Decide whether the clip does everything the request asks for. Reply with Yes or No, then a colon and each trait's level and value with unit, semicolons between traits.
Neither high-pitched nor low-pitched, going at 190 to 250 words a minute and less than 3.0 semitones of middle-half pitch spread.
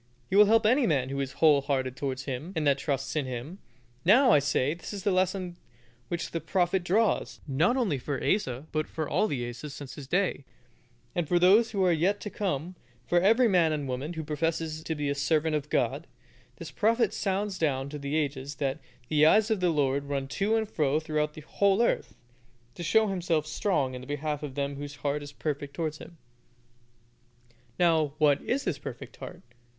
No: medium, 155 Hz; average, 200 wpm; average, 4.8 semitones